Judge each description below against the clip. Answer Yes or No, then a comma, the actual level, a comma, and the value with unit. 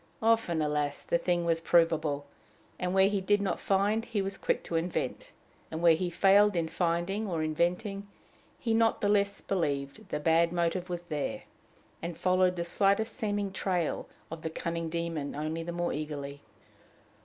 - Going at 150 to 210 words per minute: Yes, average, 170 wpm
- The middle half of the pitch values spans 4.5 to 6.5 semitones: No, average, 3.3 semitones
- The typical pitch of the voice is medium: Yes, medium, 175 Hz